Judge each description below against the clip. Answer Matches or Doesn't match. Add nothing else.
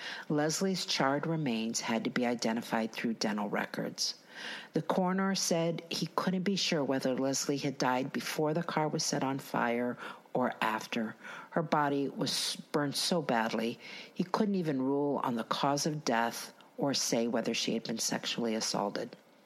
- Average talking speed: Matches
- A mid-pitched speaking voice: Matches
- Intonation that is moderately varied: Matches